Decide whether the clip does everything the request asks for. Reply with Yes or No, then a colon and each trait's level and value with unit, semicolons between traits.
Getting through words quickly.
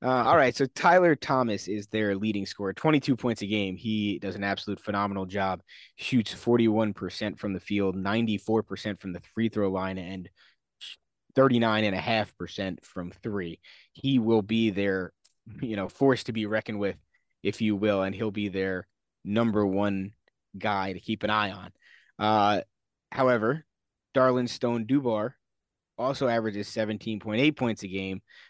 No: average, 150 wpm